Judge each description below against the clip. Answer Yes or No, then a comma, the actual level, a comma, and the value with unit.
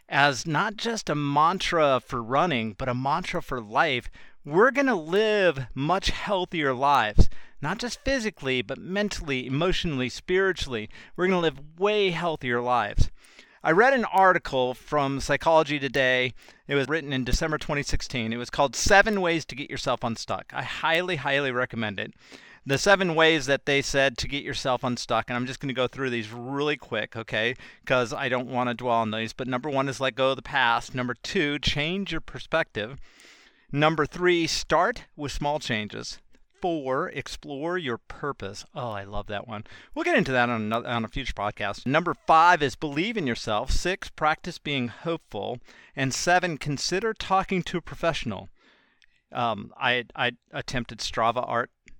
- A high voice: No, medium, 140 Hz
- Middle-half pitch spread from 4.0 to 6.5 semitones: Yes, average, 5.1 semitones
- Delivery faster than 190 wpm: No, average, 170 wpm